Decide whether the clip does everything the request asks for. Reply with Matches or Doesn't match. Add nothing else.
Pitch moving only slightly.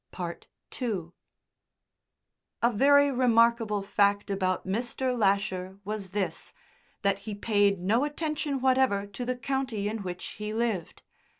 Doesn't match